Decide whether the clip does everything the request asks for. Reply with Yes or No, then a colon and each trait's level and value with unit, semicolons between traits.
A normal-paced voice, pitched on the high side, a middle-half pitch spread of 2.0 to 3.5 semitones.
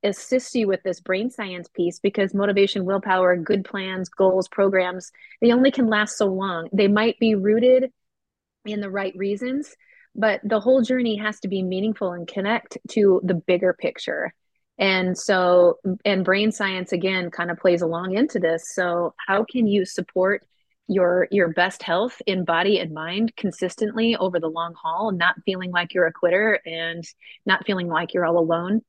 Yes: average, 175 wpm; high, 195 Hz; average, 3.2 semitones